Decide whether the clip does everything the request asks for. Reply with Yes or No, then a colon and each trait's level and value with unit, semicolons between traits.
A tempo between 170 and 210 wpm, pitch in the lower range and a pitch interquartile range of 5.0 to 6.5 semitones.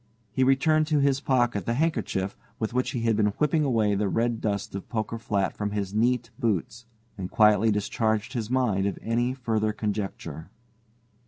No: average, 175 wpm; low, 115 Hz; average, 3.4 semitones